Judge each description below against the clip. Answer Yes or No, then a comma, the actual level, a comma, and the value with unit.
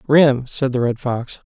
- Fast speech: No, average, 195 wpm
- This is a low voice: Yes, low, 130 Hz